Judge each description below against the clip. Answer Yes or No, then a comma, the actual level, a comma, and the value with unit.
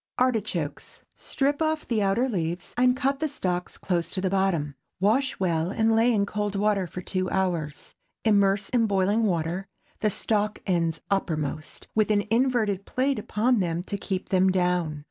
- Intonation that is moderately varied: Yes, average, 3.9 semitones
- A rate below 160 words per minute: No, average, 165 wpm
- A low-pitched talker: No, high, 195 Hz